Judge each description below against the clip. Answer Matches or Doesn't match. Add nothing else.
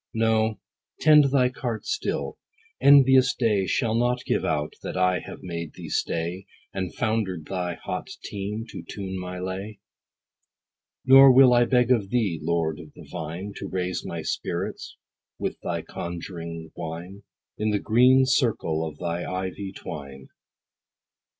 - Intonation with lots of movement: Matches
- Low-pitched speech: Matches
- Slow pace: Doesn't match